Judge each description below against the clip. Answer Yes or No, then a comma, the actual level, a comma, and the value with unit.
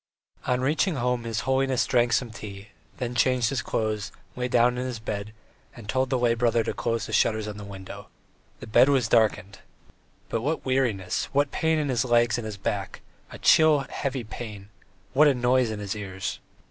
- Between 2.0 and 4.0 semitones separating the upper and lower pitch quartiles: Yes, average, 3.3 semitones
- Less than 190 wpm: No, average, 195 wpm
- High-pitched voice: No, low, 120 Hz